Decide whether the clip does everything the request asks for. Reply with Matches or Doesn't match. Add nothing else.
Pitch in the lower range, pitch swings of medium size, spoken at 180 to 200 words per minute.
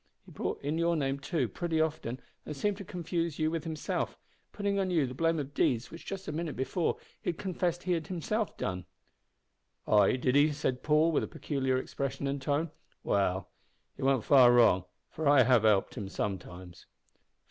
Doesn't match